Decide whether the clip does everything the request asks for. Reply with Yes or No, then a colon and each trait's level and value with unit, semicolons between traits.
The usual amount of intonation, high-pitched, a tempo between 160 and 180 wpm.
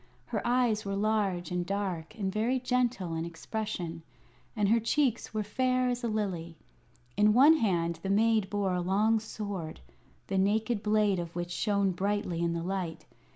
Yes: average, 3.8 semitones; high, 205 Hz; average, 170 wpm